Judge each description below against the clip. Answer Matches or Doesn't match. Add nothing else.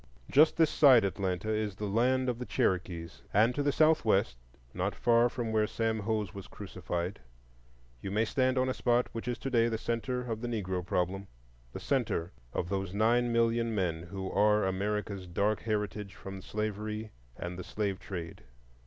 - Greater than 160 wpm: Matches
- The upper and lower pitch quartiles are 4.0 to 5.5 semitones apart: Doesn't match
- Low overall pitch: Matches